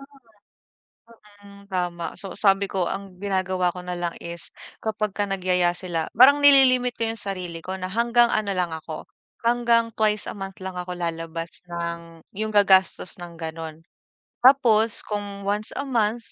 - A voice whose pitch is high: Yes, high, 195 Hz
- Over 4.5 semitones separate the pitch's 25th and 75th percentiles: No, average, 3.7 semitones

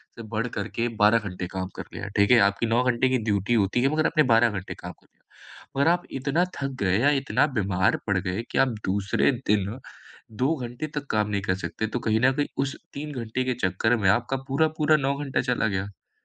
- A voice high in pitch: No, low, 115 Hz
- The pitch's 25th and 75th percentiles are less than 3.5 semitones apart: No, average, 5.1 semitones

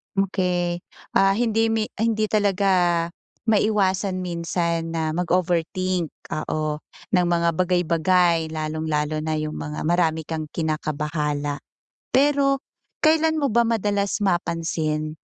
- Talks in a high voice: No, medium, 175 Hz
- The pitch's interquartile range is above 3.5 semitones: Yes, average, 4.1 semitones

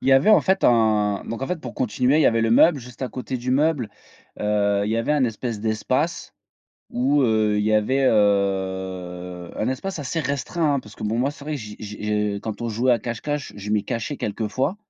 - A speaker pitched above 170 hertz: No, low, 115 Hz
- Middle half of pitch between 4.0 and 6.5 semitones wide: Yes, average, 4.3 semitones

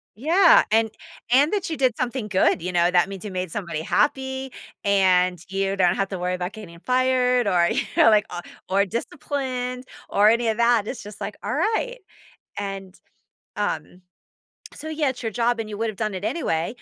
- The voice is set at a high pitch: Yes, high, 215 Hz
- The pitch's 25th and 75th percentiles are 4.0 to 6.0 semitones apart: Yes, average, 5.2 semitones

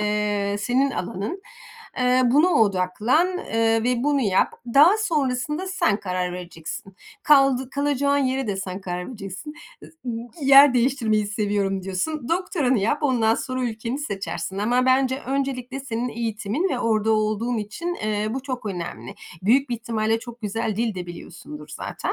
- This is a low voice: No, high, 235 Hz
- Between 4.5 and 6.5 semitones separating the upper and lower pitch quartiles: Yes, average, 4.9 semitones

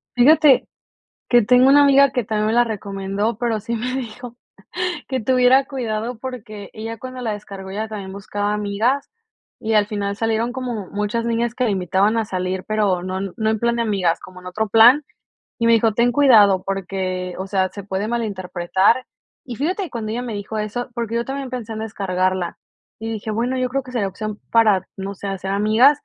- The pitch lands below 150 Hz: No, high, 220 Hz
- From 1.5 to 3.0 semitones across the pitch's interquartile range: No, average, 3.4 semitones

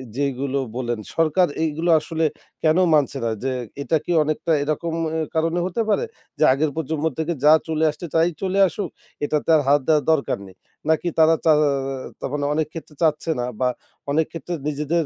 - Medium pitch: Yes, medium, 155 Hz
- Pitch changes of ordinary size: No, narrow, 2.0 semitones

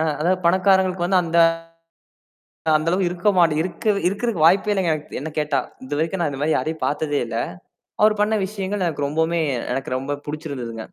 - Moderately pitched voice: Yes, medium, 170 Hz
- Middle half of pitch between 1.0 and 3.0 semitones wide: No, average, 4.0 semitones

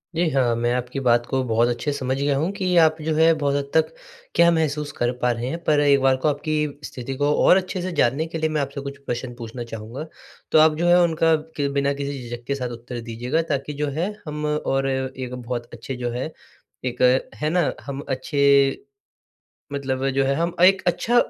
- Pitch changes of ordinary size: Yes, average, 3.7 semitones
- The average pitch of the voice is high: No, medium, 140 Hz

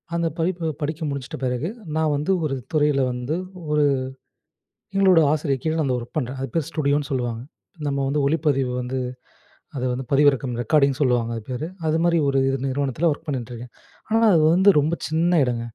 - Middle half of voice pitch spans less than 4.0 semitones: Yes, average, 3.6 semitones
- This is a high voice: No, medium, 145 Hz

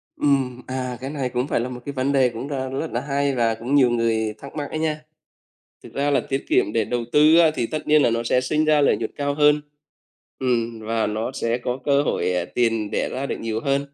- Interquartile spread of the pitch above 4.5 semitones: No, average, 3.5 semitones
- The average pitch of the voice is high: No, low, 130 Hz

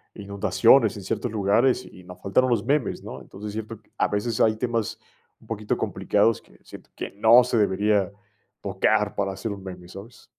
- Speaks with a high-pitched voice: No, low, 105 Hz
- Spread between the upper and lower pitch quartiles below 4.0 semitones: Yes, narrow, 2.6 semitones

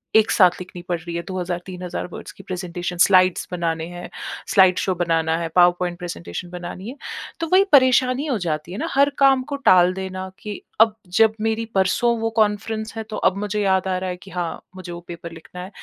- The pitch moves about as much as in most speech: Yes, average, 3.6 semitones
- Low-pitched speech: No, medium, 185 Hz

